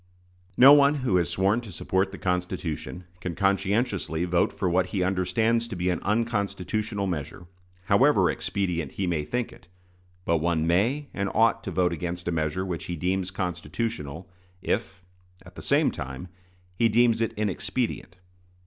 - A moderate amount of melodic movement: Yes, average, 4.0 semitones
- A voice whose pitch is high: No, very low, 95 Hz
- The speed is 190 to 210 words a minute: No, average, 160 wpm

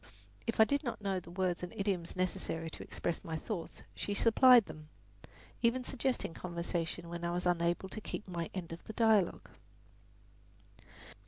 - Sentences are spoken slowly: No, average, 170 wpm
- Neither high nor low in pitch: Yes, medium, 180 Hz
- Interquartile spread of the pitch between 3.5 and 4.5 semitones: Yes, average, 4.2 semitones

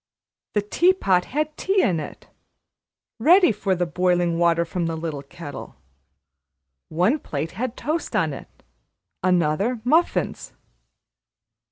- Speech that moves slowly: Yes, slow, 125 wpm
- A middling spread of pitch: No, wide, 7.3 semitones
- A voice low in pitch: No, medium, 180 Hz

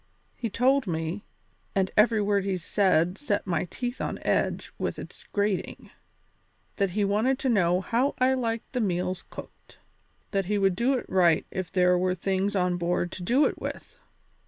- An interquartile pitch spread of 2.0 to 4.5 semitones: Yes, average, 4.2 semitones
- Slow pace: No, average, 180 wpm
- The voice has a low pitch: No, high, 195 Hz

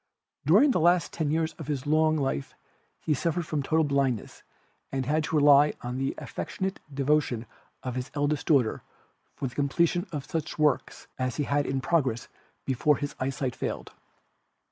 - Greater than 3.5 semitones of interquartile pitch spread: No, average, 2.9 semitones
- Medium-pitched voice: Yes, medium, 145 Hz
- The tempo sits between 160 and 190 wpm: Yes, average, 165 wpm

